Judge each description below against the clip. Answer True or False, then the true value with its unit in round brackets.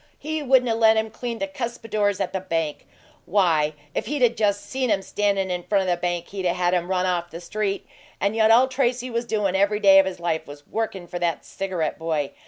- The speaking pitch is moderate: False (200 Hz)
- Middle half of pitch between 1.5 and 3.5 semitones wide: False (4.3 semitones)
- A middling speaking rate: False (230 wpm)